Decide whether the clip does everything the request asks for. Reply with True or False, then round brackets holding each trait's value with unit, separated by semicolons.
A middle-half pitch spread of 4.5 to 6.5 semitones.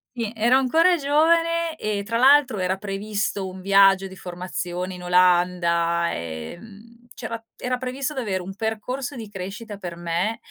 True (5.4 semitones)